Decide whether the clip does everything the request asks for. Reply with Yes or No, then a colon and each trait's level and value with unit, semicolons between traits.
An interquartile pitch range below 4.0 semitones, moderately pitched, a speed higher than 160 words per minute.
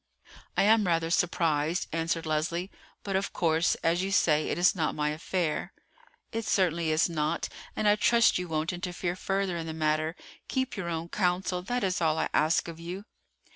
Yes: average, 2.8 semitones; medium, 170 Hz; average, 185 wpm